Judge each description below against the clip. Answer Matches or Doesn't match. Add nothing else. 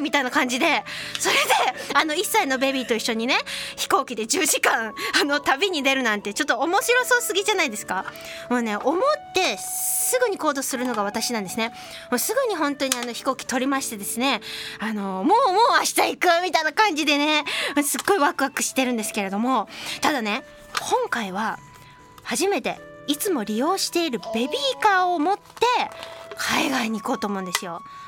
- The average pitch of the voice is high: Matches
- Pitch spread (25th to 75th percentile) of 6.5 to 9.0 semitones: Matches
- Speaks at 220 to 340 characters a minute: Doesn't match